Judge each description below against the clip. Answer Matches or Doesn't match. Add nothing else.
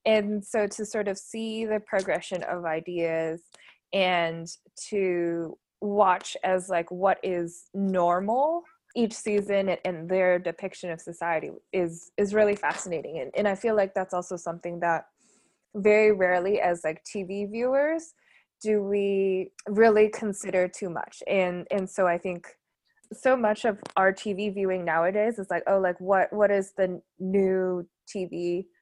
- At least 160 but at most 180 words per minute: Doesn't match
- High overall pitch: Matches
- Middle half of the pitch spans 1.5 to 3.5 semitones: Matches